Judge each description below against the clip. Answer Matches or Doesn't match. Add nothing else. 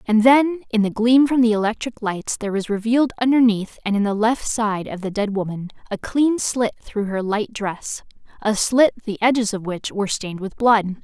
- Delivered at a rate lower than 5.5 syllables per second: Matches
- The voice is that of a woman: Matches